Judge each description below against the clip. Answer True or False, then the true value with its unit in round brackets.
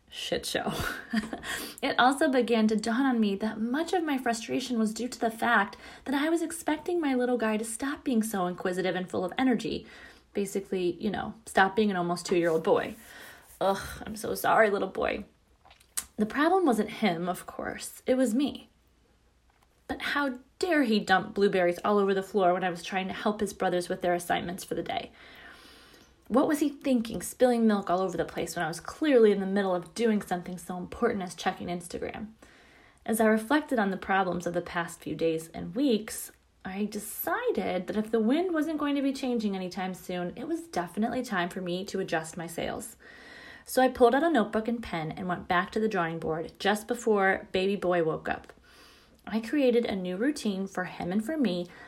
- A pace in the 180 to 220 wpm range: True (200 wpm)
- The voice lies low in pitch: False (215 Hz)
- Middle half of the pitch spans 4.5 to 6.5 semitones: True (5.6 semitones)